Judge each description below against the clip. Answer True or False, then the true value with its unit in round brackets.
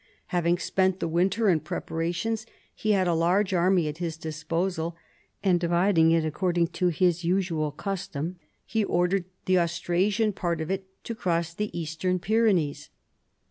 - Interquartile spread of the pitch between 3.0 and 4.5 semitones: False (2.5 semitones)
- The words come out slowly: False (150 wpm)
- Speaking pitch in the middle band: True (175 Hz)